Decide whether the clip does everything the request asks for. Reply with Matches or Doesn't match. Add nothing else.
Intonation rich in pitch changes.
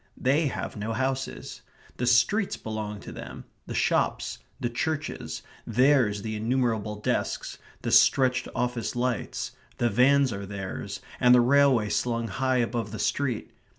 Doesn't match